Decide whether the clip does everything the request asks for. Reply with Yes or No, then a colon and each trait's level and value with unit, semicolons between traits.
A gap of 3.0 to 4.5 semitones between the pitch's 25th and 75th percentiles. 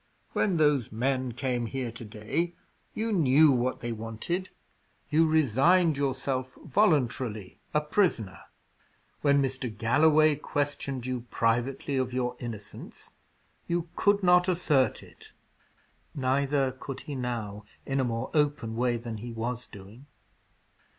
Yes: average, 4.1 semitones